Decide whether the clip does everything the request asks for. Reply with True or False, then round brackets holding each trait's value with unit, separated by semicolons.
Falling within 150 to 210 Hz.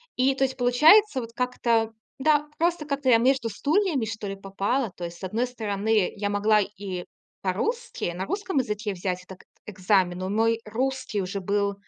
False (220 Hz)